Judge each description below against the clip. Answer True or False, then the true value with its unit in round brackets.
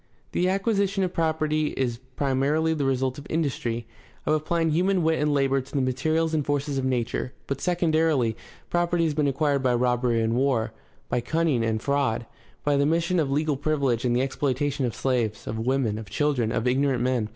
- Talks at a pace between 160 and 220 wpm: True (190 wpm)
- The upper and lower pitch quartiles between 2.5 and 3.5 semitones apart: False (4.1 semitones)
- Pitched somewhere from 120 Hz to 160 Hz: True (140 Hz)